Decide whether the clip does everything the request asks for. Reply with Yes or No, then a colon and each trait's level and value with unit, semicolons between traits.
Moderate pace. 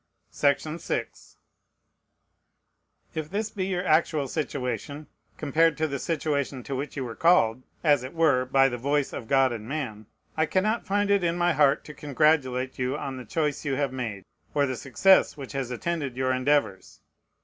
Yes: average, 170 wpm